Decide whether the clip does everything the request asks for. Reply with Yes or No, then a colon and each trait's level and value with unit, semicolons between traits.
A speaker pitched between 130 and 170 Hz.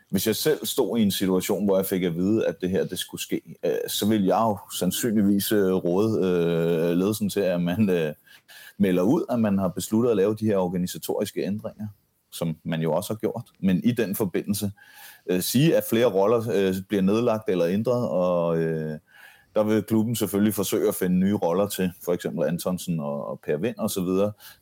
No: very low, 95 Hz